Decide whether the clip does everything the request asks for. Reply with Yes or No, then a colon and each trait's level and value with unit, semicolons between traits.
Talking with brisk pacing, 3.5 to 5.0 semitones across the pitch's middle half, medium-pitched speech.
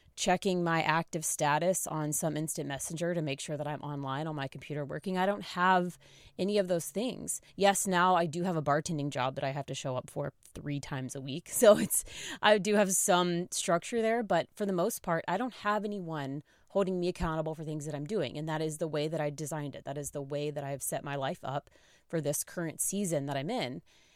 Yes: fast, 235 wpm; average, 4.0 semitones; medium, 160 Hz